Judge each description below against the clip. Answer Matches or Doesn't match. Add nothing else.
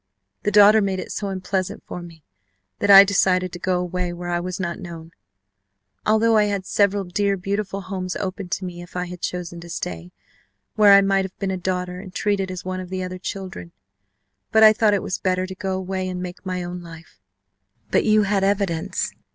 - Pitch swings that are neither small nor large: Doesn't match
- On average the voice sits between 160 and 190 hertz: Matches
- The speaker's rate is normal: Doesn't match